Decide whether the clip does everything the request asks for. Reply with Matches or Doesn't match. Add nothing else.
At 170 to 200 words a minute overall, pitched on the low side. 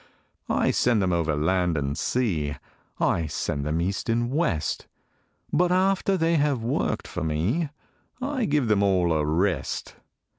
Doesn't match